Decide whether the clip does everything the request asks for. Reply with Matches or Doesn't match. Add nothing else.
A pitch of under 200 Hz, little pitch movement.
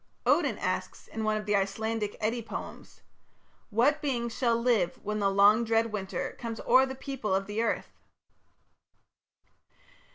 Doesn't match